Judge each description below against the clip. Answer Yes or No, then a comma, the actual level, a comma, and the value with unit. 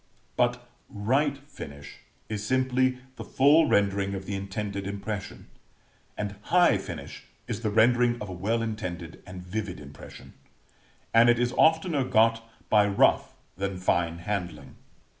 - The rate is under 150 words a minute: Yes, average, 140 wpm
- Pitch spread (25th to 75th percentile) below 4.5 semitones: Yes, average, 4.0 semitones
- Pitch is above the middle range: No, low, 105 Hz